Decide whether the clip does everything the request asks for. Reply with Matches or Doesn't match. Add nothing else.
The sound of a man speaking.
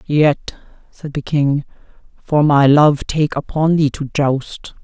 Doesn't match